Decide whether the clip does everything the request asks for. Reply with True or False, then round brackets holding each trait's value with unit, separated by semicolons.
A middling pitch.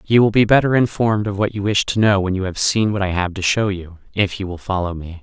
False (100 Hz)